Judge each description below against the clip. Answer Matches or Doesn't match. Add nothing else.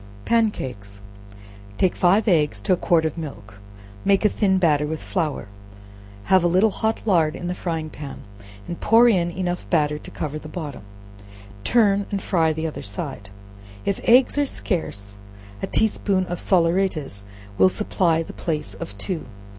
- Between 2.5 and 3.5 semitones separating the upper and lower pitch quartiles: Doesn't match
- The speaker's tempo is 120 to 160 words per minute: Doesn't match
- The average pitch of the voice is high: Doesn't match